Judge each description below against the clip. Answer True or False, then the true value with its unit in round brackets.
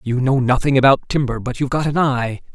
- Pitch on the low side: True (130 Hz)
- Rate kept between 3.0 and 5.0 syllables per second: False (6.0 syllables/s)